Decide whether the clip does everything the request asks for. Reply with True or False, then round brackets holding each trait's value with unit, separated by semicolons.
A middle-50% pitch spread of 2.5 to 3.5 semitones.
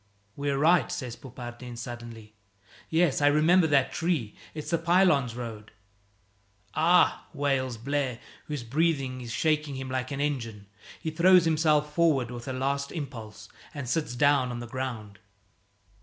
False (4.2 semitones)